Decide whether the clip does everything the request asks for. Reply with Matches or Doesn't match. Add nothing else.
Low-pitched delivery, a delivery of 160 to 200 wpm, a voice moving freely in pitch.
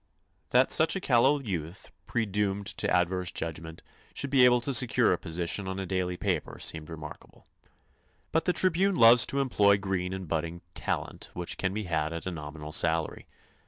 Matches